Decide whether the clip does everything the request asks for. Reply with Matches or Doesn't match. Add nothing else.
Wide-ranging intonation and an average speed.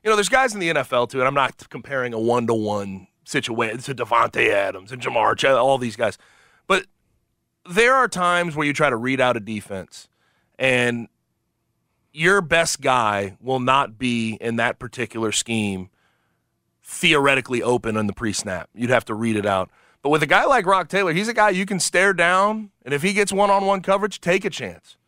Doesn't match